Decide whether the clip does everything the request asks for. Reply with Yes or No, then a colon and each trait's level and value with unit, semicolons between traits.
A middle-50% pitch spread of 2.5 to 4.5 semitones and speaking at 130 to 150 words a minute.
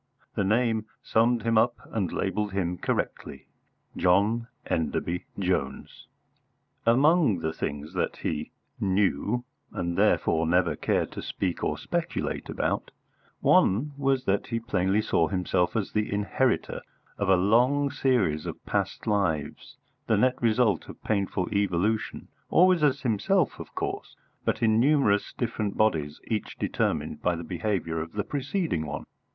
No: average, 5.0 semitones; average, 140 wpm